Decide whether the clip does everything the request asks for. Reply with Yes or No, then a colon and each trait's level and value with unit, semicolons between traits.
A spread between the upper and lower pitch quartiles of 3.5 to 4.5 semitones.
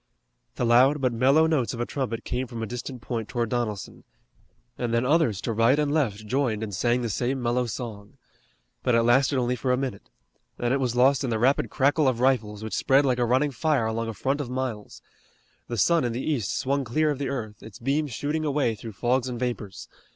No: average, 2.9 semitones